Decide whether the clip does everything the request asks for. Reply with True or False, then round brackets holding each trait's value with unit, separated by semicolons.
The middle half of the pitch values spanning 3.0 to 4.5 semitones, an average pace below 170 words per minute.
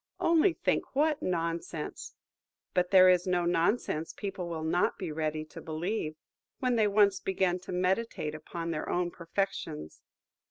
True (3.3 semitones; 150 wpm)